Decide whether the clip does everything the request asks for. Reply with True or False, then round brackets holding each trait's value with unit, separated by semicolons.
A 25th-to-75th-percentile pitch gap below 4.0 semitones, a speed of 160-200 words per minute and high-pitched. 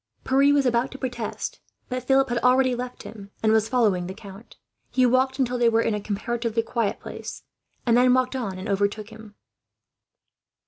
True (2.9 semitones; 185 wpm; 235 Hz)